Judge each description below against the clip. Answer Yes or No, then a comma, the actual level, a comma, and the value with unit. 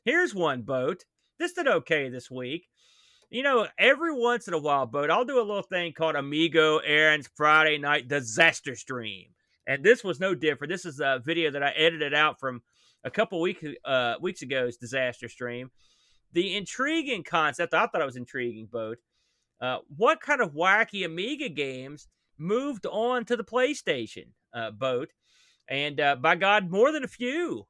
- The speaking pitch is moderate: Yes, medium, 155 Hz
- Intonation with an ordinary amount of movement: No, wide, 7.2 semitones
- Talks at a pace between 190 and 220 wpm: No, average, 175 wpm